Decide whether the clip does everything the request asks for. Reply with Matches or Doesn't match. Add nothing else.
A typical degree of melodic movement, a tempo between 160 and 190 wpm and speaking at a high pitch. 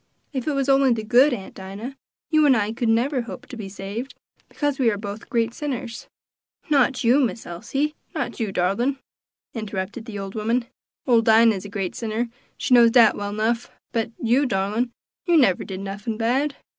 Matches